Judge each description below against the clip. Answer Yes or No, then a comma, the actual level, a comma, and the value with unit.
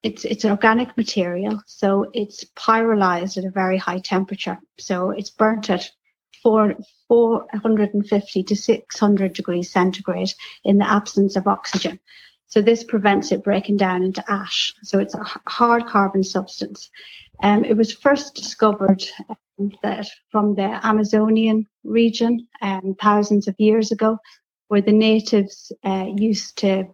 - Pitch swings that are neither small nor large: No, narrow, 2.2 semitones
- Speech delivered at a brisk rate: No, average, 145 wpm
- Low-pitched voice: No, high, 205 Hz